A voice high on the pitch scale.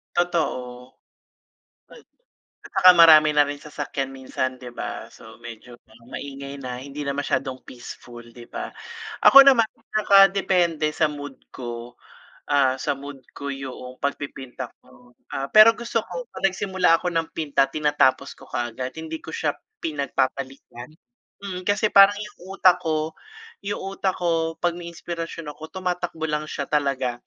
No: medium, 150 Hz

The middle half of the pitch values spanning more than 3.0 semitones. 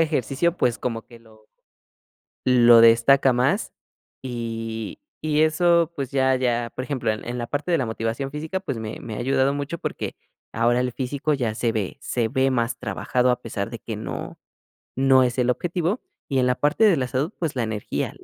Yes: average, 3.6 semitones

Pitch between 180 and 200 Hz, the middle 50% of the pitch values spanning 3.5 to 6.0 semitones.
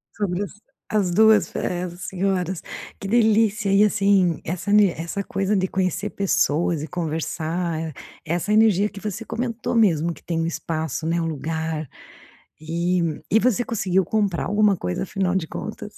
Yes: medium, 185 Hz; average, 3.8 semitones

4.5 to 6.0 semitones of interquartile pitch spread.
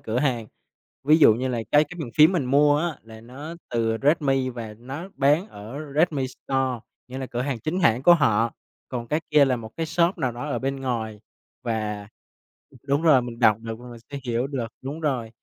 No: average, 4.1 semitones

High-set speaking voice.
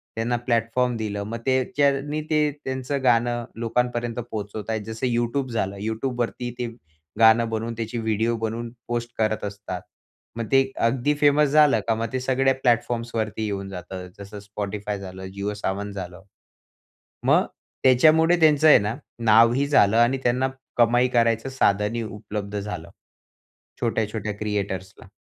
No: low, 115 Hz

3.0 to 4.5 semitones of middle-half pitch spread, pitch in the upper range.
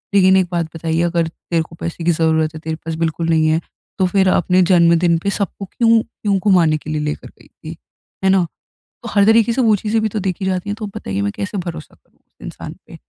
No: average, 3.4 semitones; medium, 175 Hz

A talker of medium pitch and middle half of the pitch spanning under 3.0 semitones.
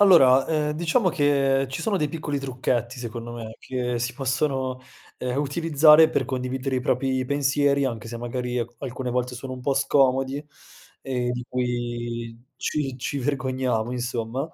No: low, 130 Hz; narrow, 2.4 semitones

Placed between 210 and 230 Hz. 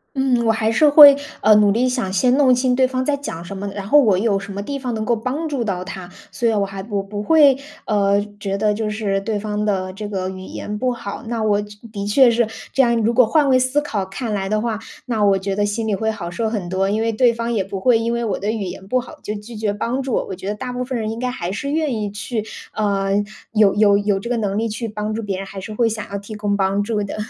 Yes: high, 215 Hz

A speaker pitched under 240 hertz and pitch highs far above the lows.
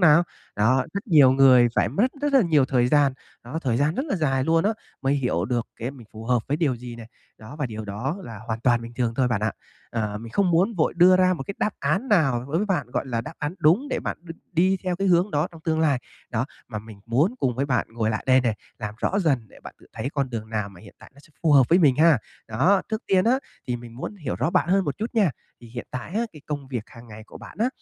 Yes: low, 135 Hz; wide, 6.5 semitones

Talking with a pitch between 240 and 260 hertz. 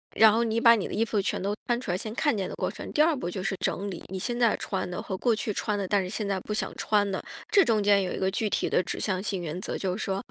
No: high, 205 Hz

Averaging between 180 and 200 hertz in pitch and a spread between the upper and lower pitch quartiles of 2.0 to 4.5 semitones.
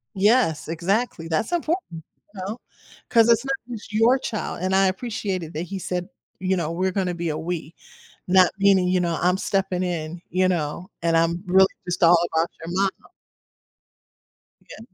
Yes: medium, 185 Hz; average, 3.1 semitones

